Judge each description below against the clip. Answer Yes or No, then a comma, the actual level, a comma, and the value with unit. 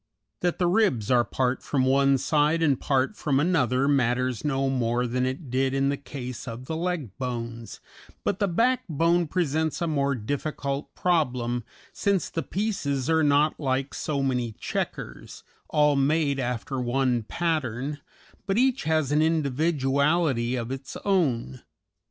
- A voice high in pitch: No, medium, 140 Hz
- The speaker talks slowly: No, average, 150 wpm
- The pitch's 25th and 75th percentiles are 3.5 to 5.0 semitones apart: Yes, average, 4.0 semitones